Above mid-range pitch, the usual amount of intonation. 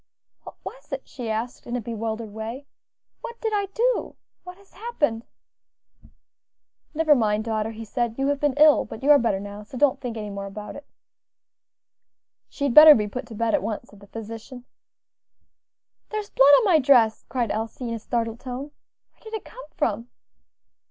Yes: high, 240 Hz; average, 5.0 semitones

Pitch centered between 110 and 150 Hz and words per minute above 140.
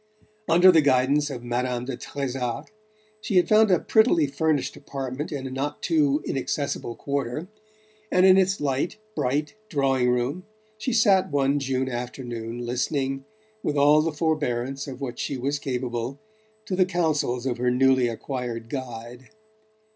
Yes: low, 135 Hz; average, 150 wpm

